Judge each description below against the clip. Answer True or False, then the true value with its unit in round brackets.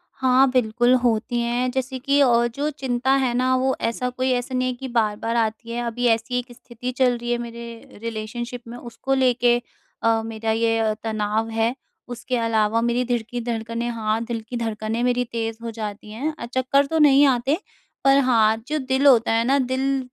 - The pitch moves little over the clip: True (2.0 semitones)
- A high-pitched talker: True (240 Hz)